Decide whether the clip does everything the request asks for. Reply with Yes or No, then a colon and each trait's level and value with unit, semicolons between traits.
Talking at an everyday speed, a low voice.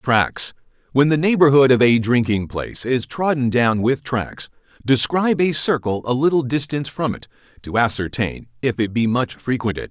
Yes: average, 165 wpm; low, 125 Hz